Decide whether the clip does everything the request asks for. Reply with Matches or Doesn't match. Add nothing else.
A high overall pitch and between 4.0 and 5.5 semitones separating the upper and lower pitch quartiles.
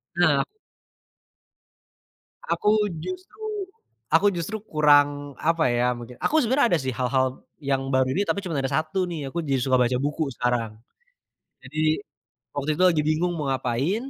Doesn't match